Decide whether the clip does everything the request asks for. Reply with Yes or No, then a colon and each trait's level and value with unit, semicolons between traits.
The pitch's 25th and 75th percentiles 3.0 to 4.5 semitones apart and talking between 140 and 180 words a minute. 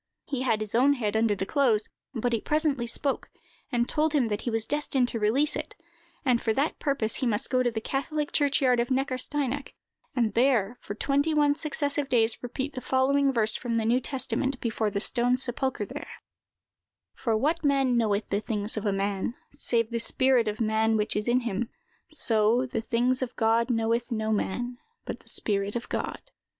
No: average, 3.4 semitones; average, 195 wpm